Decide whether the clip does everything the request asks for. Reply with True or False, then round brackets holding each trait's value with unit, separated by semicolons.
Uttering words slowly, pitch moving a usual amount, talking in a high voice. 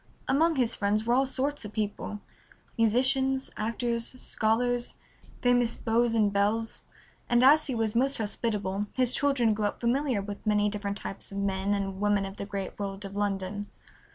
False (170 wpm; 3.3 semitones; 220 Hz)